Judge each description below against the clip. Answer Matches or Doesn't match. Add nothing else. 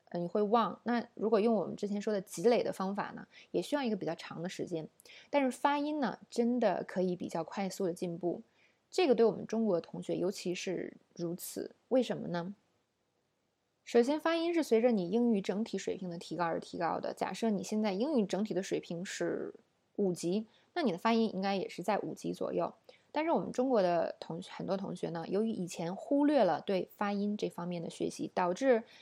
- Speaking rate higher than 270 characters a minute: Matches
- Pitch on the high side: Matches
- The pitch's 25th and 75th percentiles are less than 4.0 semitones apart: Doesn't match